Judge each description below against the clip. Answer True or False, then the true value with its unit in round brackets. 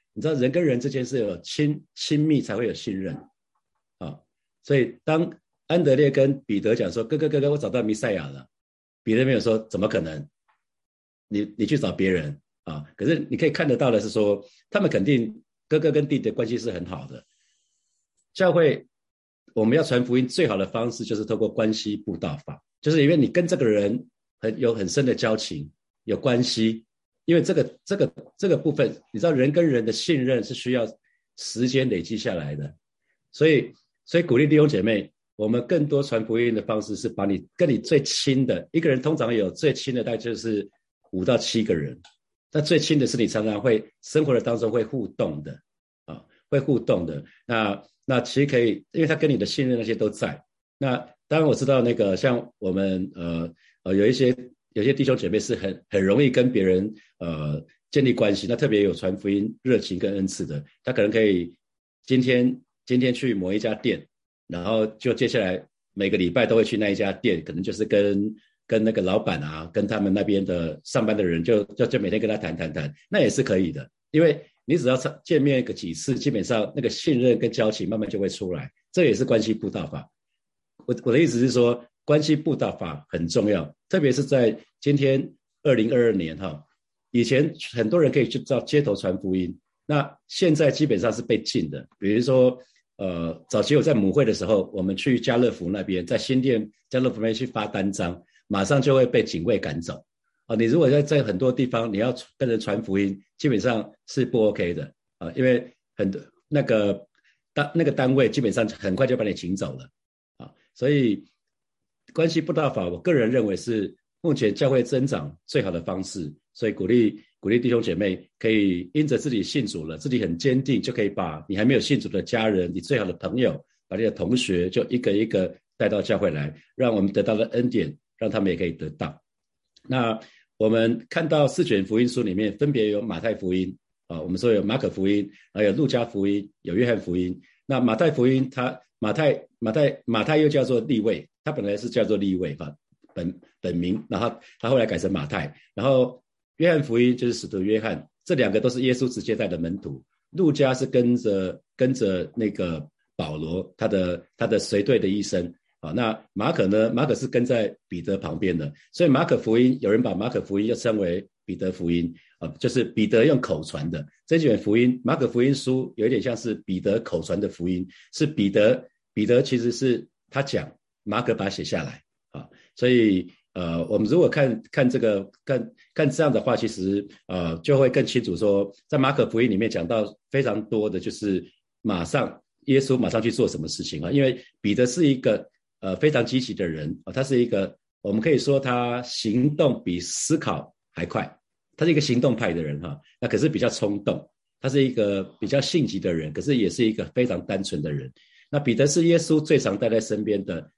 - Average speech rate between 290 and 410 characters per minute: True (295 characters per minute)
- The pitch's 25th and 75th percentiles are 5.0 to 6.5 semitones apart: True (5.3 semitones)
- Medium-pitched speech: False (115 Hz)